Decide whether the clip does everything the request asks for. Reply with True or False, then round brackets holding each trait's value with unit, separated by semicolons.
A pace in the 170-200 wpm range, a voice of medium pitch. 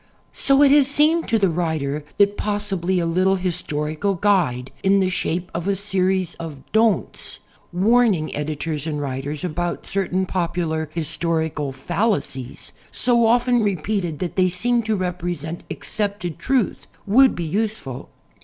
False (145 wpm; 180 Hz)